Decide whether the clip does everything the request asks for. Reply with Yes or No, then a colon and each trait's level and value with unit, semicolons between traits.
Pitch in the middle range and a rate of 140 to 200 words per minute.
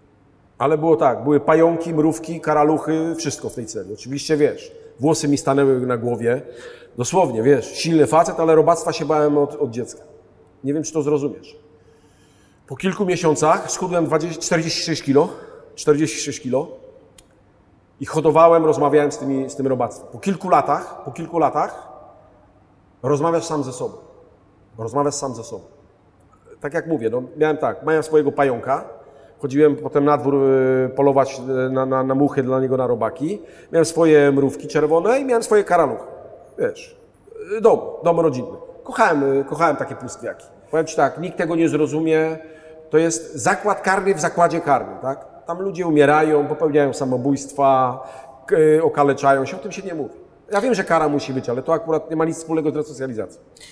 Yes: medium, 150 Hz; fast, 160 wpm